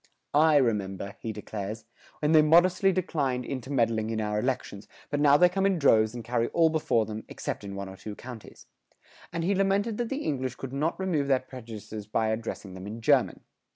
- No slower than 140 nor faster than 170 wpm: No, average, 200 wpm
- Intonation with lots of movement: Yes, wide, 6.5 semitones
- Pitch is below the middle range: Yes, low, 125 Hz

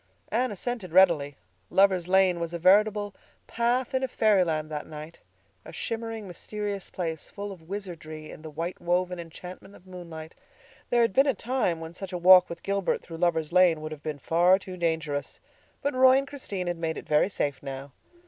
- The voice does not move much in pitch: No, average, 4.0 semitones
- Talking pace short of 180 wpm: No, average, 185 wpm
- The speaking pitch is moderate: Yes, medium, 180 Hz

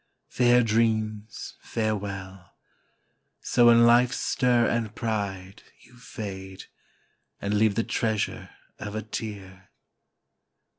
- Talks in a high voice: No, low, 110 Hz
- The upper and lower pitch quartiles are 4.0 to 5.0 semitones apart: No, average, 2.9 semitones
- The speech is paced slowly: Yes, slow, 100 wpm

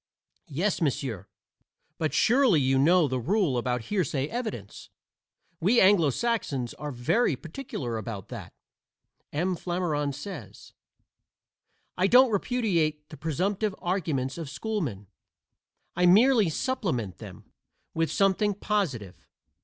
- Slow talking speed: Yes, slow, 115 wpm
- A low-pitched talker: No, medium, 165 Hz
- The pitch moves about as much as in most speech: No, wide, 7.3 semitones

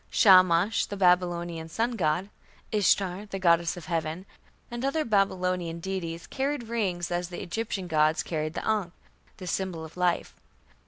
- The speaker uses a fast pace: No, average, 150 wpm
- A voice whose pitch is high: No, medium, 180 Hz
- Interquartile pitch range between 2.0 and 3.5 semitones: Yes, average, 3.0 semitones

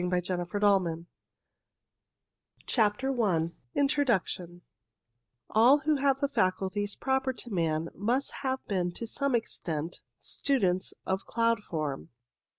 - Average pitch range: No, wide, 6.8 semitones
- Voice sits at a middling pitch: No, high, 205 Hz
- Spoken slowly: Yes, slow, 120 wpm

